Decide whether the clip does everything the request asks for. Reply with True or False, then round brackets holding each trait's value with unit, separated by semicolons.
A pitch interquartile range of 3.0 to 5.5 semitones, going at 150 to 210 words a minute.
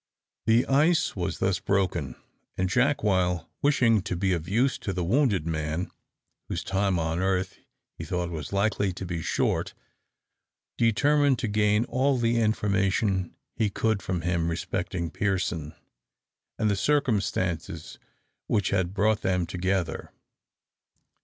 False (3.8 semitones; 135 wpm)